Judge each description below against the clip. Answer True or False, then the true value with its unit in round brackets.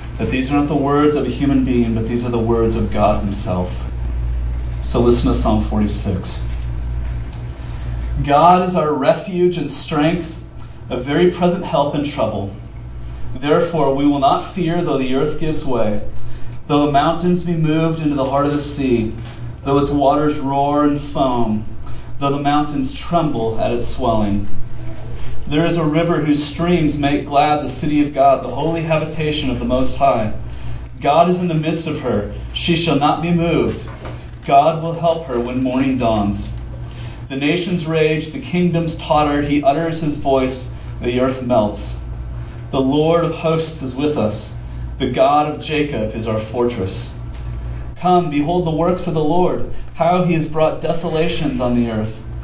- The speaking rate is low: False (170 wpm)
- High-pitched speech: False (140 Hz)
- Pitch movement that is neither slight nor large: False (5.7 semitones)